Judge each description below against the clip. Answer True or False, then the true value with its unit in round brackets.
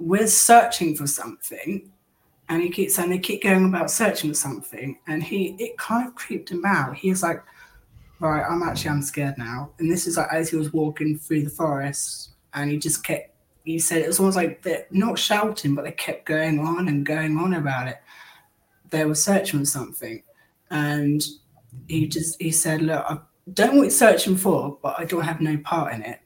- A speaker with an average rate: False (210 wpm)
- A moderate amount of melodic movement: True (3.6 semitones)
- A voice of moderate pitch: True (160 Hz)